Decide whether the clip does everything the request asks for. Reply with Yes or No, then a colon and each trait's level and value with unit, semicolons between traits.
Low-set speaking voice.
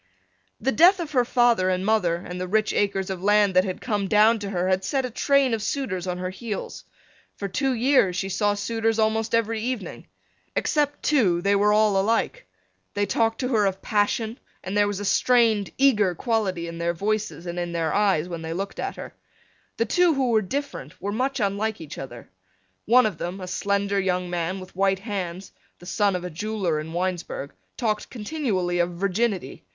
No: high, 205 Hz